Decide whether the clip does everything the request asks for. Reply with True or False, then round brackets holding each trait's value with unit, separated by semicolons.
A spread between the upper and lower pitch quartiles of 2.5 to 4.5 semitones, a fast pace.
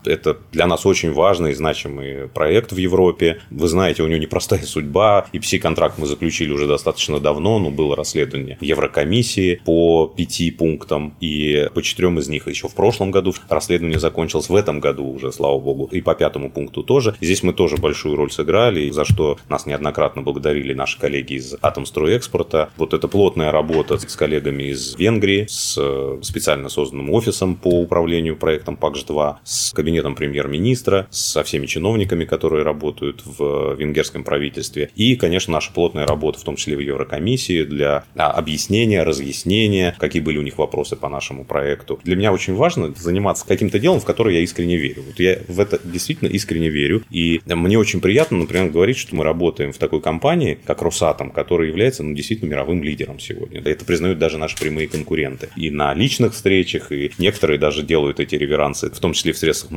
True (4.0 semitones; 180 wpm)